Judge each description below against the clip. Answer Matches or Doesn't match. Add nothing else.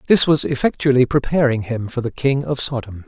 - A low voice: Matches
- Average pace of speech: Matches